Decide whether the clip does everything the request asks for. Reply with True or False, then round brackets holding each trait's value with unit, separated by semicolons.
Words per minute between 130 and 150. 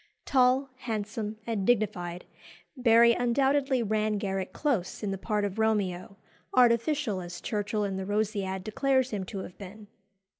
True (145 wpm)